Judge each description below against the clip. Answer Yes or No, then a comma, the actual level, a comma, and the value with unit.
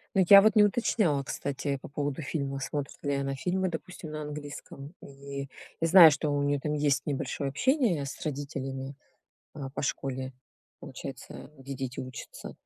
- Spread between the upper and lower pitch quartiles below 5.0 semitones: Yes, narrow, 2.4 semitones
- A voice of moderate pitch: Yes, medium, 145 Hz